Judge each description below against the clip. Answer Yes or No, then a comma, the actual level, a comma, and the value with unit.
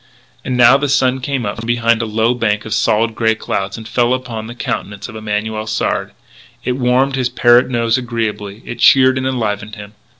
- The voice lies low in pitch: Yes, low, 115 Hz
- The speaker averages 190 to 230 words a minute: Yes, average, 200 wpm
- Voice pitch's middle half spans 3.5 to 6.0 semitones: No, narrow, 2.5 semitones